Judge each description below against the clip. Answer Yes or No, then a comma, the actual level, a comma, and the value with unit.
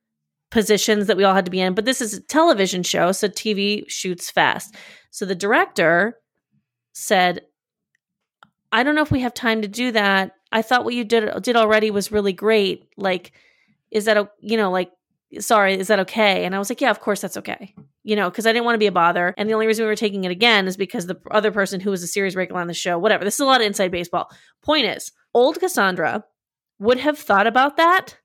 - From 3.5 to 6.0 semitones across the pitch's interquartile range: No, average, 3.1 semitones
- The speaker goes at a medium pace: No, fast, 235 wpm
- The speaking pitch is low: No, high, 205 Hz